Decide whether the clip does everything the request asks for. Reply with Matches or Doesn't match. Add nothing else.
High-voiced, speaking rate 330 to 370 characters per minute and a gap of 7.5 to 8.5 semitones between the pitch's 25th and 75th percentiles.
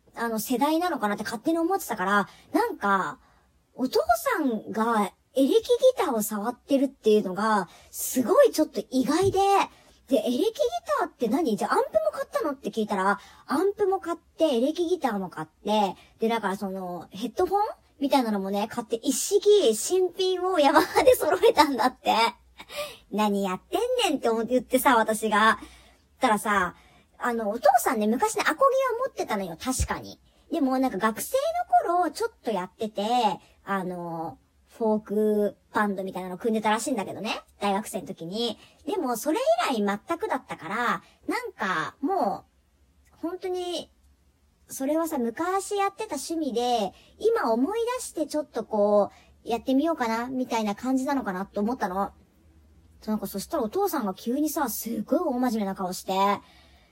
Matches